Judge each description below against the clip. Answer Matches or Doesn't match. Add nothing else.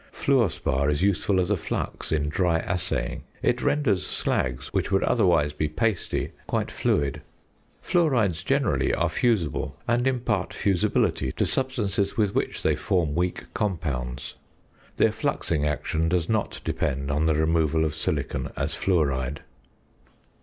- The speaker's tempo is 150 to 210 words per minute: Doesn't match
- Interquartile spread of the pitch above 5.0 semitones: Matches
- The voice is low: Matches